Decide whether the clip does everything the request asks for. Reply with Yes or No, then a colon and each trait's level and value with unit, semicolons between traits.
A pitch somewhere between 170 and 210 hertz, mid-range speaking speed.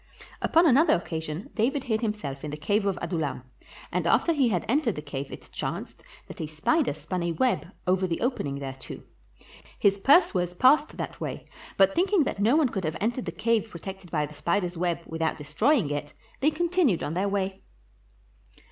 Yes: high, 190 Hz; average, 185 wpm